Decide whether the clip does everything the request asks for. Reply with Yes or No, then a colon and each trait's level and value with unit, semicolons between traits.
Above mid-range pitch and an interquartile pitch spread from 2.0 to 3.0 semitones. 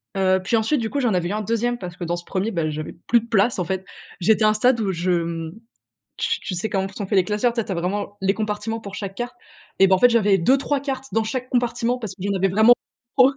No: high, 210 Hz; average, 3.8 semitones